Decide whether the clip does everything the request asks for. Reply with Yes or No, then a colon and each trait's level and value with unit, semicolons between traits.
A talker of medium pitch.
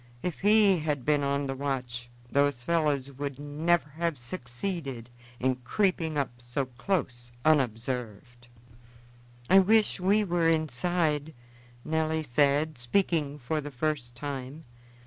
Yes: medium, 145 Hz